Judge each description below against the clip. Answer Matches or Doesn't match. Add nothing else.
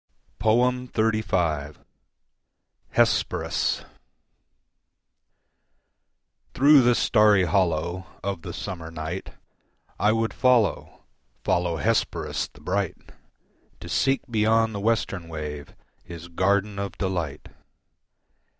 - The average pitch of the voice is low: Matches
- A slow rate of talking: Matches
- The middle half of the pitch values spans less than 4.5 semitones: Doesn't match